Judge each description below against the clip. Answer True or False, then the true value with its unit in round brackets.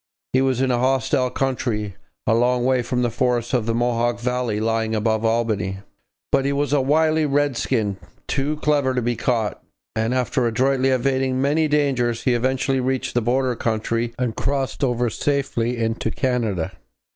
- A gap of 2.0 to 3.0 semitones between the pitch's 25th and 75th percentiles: True (2.5 semitones)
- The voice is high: False (125 Hz)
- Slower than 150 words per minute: False (170 wpm)